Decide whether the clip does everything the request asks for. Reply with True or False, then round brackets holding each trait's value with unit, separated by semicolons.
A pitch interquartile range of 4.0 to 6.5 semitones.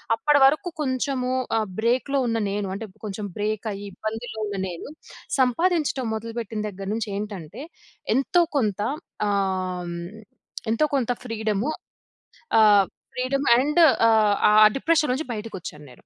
True (4.3 semitones)